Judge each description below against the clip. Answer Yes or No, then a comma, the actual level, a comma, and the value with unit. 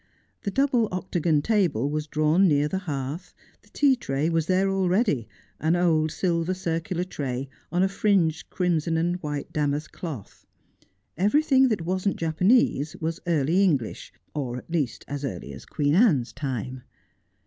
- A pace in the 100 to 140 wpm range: No, average, 150 wpm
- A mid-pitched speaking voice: Yes, medium, 165 Hz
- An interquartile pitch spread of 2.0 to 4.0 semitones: No, average, 4.4 semitones